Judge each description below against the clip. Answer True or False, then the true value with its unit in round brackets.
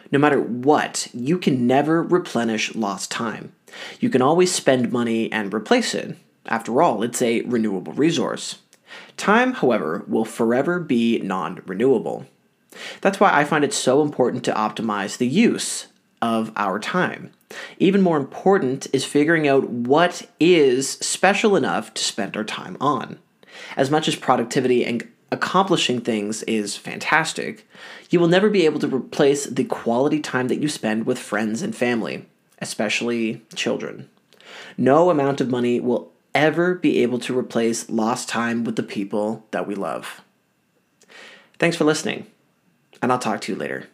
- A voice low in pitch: True (125 Hz)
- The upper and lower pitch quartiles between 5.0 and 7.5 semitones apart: True (5.6 semitones)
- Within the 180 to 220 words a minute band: False (155 wpm)